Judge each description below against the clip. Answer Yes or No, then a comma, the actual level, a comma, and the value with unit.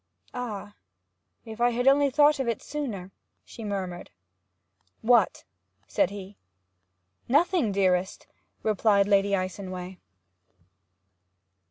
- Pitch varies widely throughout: No, average, 4.4 semitones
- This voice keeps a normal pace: No, slow, 95 wpm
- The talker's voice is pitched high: Yes, high, 205 Hz